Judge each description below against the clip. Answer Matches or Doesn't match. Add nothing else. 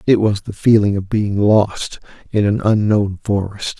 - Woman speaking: Doesn't match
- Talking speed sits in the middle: Matches